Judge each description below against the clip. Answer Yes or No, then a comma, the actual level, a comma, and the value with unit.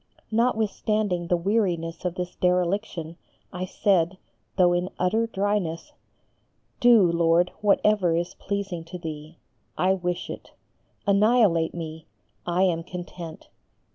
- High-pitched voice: No, medium, 180 Hz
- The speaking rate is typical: No, slow, 115 wpm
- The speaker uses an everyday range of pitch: Yes, average, 3.1 semitones